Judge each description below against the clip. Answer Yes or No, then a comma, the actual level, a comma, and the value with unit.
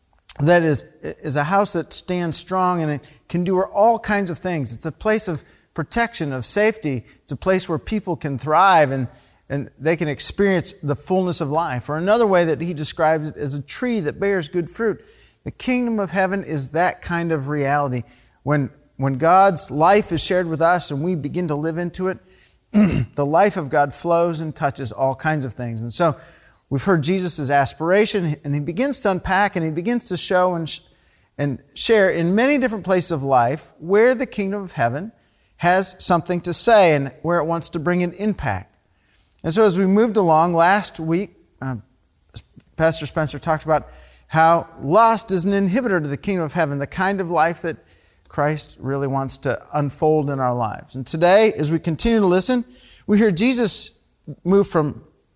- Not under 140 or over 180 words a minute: No, average, 195 wpm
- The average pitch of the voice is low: No, medium, 165 Hz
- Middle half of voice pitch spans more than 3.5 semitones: Yes, average, 5.0 semitones